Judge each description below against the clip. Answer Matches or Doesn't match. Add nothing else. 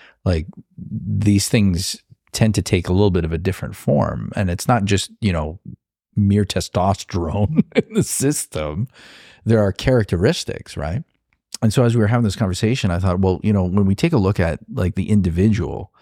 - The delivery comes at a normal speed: Matches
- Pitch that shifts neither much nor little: Matches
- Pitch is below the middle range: Matches